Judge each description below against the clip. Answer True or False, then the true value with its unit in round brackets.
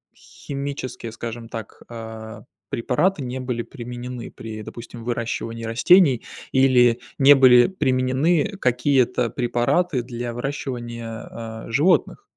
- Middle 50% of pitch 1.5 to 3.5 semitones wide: True (2.5 semitones)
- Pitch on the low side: True (125 Hz)